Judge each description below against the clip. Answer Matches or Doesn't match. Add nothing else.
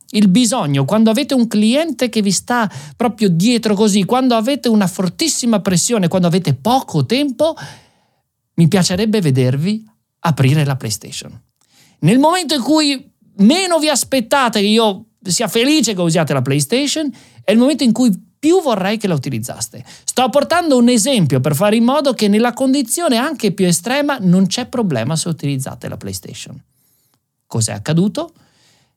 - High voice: Matches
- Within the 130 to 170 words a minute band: Matches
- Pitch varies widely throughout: Matches